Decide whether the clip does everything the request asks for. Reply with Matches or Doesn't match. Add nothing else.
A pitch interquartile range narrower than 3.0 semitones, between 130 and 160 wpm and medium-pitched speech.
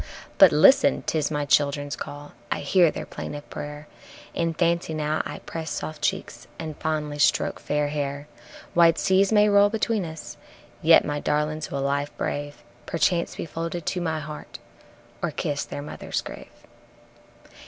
Matches